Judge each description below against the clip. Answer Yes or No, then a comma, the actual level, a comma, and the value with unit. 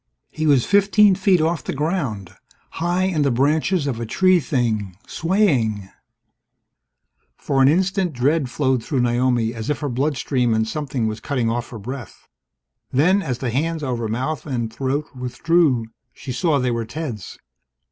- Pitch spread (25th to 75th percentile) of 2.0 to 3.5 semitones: No, average, 5.2 semitones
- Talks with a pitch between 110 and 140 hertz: Yes, low, 135 Hz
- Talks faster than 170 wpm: No, average, 165 wpm